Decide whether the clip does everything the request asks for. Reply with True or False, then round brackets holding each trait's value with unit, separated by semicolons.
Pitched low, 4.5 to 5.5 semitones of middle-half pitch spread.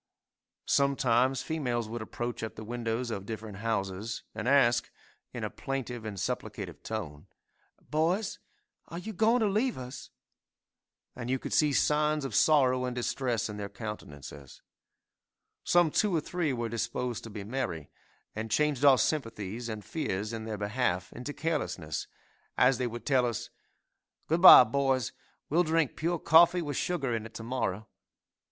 True (125 Hz; 5.2 semitones)